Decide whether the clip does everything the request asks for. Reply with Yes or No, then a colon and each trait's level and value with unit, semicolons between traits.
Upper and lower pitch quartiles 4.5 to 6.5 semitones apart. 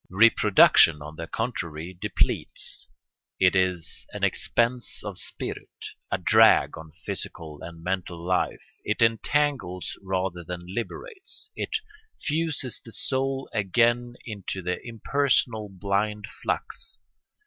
Yes: average, 5.0 semitones